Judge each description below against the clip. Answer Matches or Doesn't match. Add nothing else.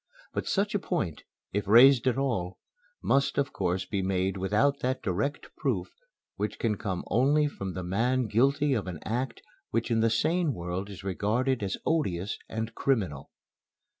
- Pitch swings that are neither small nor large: Doesn't match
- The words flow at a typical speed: Matches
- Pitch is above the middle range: Doesn't match